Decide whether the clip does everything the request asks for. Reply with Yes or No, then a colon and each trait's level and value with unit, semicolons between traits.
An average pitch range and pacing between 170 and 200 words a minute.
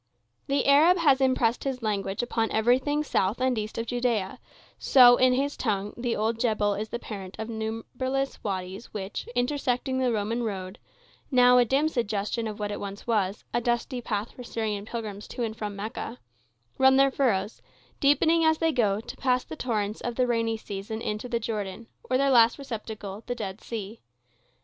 Yes: average, 3.5 semitones; average, 180 wpm